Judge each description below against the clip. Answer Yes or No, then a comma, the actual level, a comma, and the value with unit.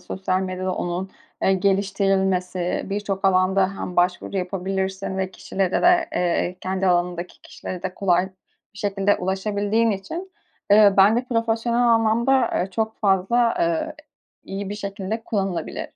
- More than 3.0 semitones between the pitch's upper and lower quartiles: No, narrow, 2.4 semitones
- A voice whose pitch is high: Yes, high, 195 Hz